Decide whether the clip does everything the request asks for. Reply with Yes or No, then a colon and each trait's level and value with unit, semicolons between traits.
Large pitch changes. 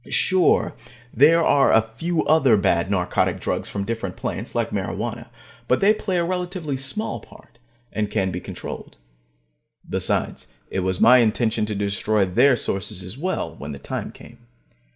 Yes: wide, 8.3 semitones